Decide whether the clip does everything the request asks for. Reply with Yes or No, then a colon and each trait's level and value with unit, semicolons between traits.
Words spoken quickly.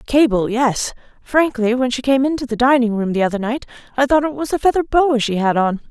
Yes: fast, 225 wpm